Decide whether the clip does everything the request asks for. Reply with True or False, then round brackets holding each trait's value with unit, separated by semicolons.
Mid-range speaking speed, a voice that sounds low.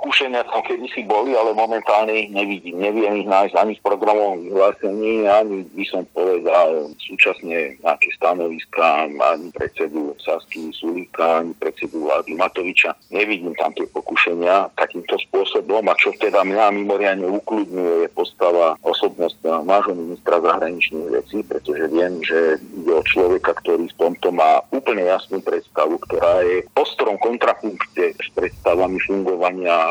True (140 wpm; 115 Hz)